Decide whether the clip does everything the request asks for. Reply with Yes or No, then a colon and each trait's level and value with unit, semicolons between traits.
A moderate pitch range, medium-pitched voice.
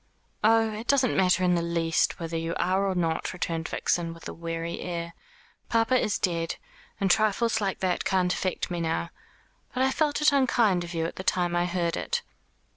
Yes: average, 4.4 semitones; medium, 180 Hz